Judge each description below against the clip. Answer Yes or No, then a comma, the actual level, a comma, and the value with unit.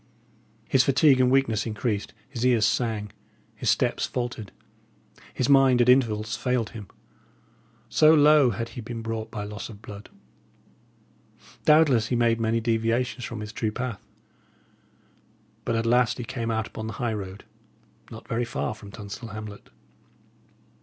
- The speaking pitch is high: No, low, 115 Hz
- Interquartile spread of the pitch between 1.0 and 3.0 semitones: Yes, narrow, 2.5 semitones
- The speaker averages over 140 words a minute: Yes, average, 150 wpm